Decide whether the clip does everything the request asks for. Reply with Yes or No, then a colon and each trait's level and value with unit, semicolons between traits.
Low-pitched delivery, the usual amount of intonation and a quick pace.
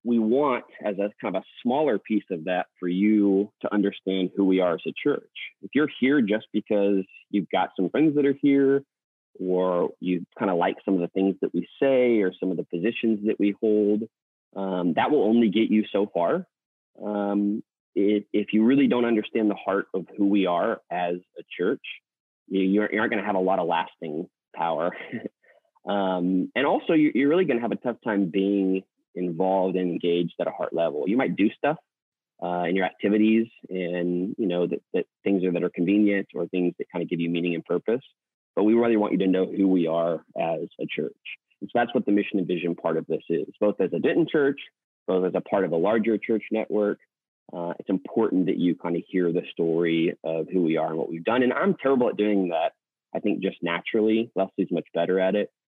Yes: low, 100 Hz; average, 3.2 semitones; fast, 225 wpm